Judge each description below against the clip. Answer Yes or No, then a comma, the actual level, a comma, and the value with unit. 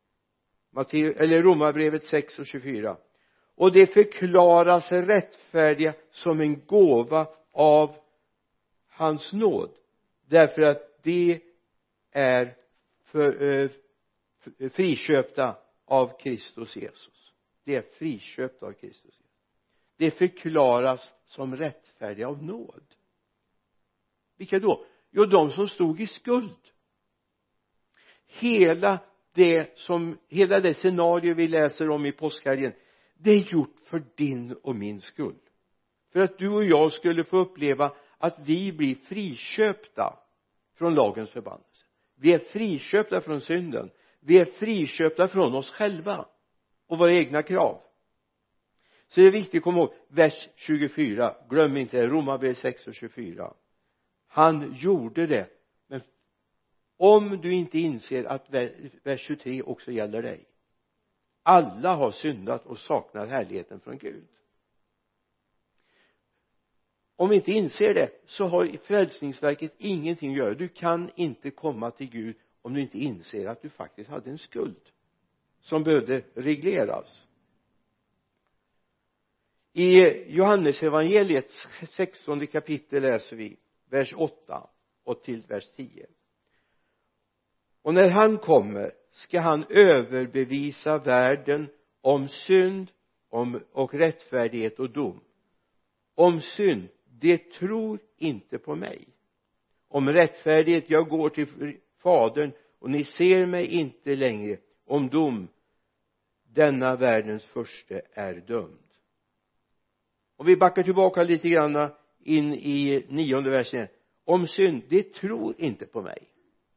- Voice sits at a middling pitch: Yes, medium, 155 Hz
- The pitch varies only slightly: No, average, 4.8 semitones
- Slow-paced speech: Yes, slow, 120 wpm